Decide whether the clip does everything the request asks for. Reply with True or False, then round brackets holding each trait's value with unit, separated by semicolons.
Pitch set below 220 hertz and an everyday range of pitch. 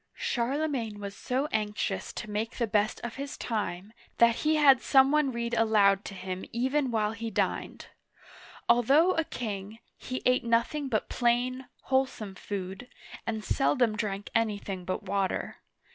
False (230 Hz; 3.8 semitones)